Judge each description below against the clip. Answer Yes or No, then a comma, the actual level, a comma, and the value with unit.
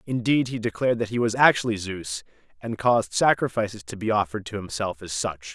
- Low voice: Yes, low, 105 Hz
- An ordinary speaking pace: Yes, average, 195 wpm